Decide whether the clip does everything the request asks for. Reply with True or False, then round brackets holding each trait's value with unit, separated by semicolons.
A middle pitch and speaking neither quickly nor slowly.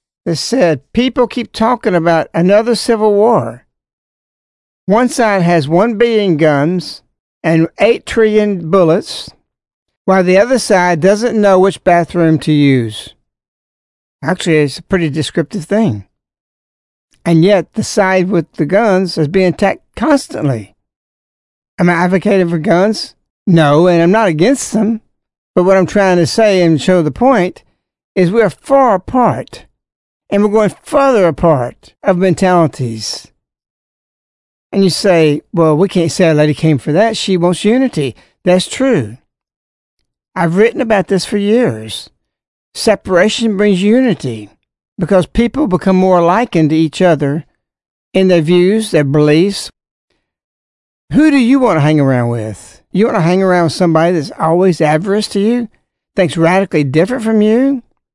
True (180 Hz; 145 wpm)